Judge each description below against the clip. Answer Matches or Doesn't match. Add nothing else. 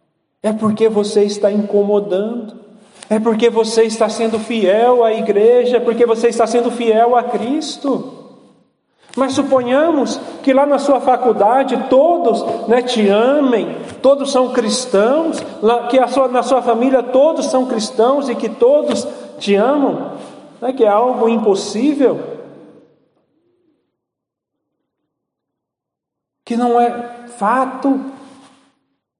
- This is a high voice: Matches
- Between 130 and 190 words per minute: Doesn't match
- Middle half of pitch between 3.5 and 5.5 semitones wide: Doesn't match